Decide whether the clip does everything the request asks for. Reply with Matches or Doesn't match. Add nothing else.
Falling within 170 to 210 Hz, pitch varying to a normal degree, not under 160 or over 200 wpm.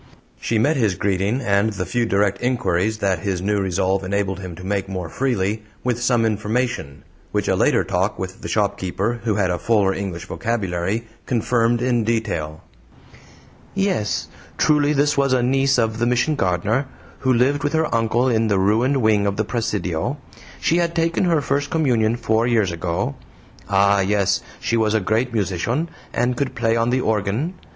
Doesn't match